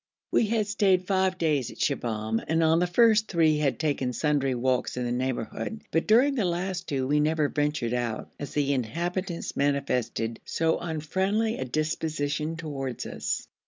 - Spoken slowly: No, average, 165 wpm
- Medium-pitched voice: Yes, medium, 155 Hz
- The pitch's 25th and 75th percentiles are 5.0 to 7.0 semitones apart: Yes, wide, 5.4 semitones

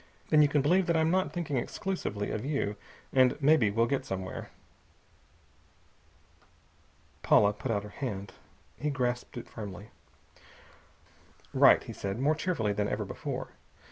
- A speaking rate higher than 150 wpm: No, average, 140 wpm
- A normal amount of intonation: No, wide, 6.5 semitones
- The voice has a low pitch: Yes, low, 125 Hz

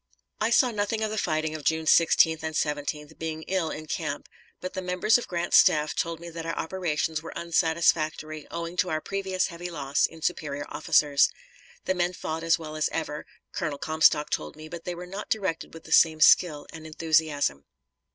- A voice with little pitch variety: Yes, narrow, 2.3 semitones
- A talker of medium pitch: Yes, medium, 160 Hz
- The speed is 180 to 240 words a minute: Yes, average, 195 wpm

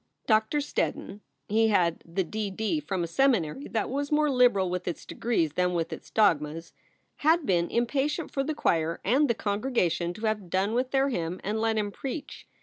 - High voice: Yes, high, 215 Hz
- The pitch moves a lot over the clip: Yes, wide, 6.9 semitones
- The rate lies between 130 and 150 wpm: No, average, 185 wpm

